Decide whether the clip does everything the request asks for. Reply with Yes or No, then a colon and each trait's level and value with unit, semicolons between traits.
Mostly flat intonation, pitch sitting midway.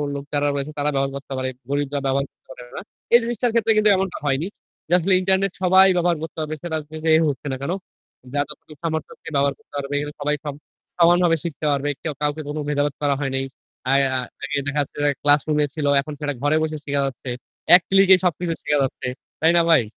No: average, 3.4 semitones; medium, 150 Hz